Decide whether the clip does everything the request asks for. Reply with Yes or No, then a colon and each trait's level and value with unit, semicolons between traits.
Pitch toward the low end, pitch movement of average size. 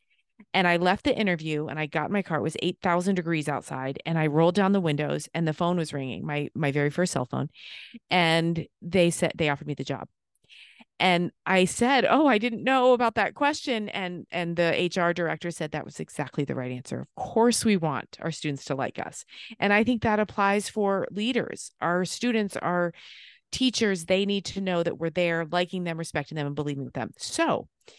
No: medium, 175 Hz; average, 4.5 semitones